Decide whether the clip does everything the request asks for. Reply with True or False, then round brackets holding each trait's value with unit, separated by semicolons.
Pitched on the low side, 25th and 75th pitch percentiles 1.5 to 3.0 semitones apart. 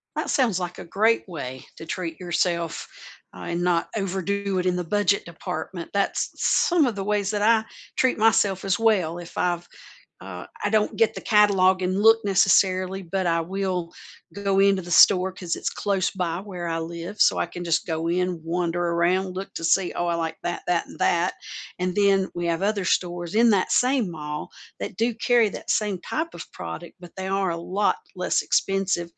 False (185 Hz; 2.7 semitones)